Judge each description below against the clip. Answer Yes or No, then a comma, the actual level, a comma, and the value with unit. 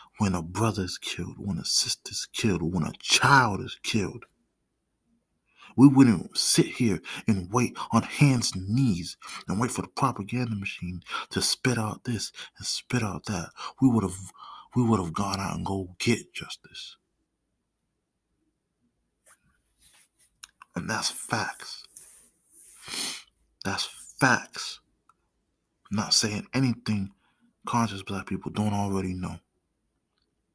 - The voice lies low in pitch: Yes, low, 105 Hz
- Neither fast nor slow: No, slow, 130 wpm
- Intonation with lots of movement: No, average, 4.4 semitones